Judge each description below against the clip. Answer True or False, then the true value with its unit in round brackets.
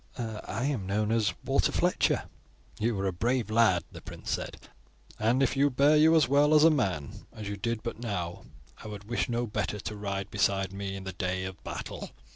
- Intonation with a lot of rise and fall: False (3.9 semitones)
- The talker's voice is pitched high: False (105 Hz)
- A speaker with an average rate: False (210 wpm)